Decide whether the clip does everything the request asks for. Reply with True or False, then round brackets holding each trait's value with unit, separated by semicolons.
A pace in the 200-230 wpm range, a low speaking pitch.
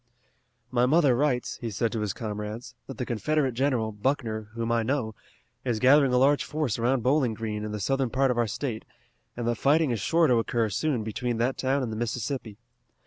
True (205 wpm; 120 Hz)